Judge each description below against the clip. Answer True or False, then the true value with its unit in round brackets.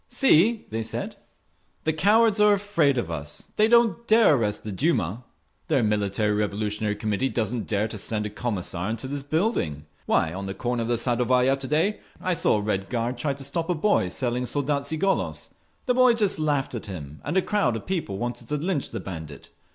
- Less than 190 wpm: False (200 wpm)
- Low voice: True (125 Hz)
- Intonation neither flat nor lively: False (7.8 semitones)